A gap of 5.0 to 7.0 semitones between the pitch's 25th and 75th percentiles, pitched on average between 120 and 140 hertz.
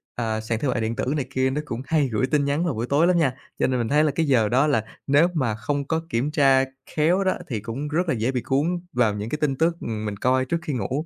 No: average, 4.5 semitones; low, 135 Hz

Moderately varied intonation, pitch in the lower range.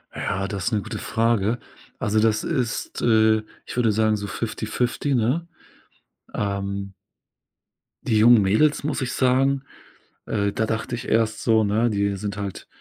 Yes: average, 3.0 semitones; low, 110 Hz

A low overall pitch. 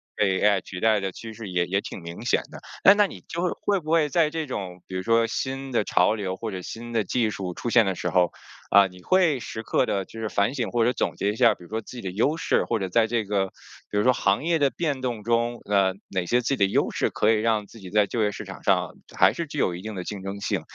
Yes: low, 110 Hz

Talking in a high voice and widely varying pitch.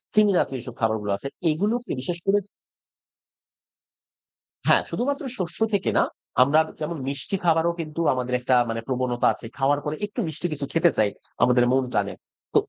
No: medium, 150 Hz; wide, 5.8 semitones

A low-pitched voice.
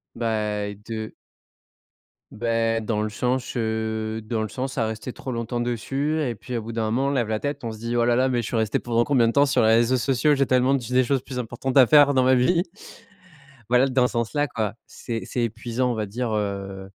Yes: low, 120 Hz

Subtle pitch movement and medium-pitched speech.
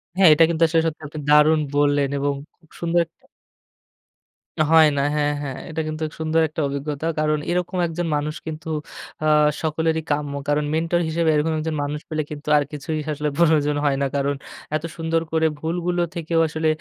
Yes: narrow, 1.6 semitones; medium, 155 Hz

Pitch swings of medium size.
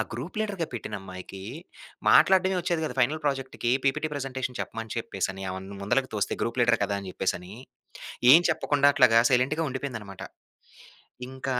No: wide, 5.7 semitones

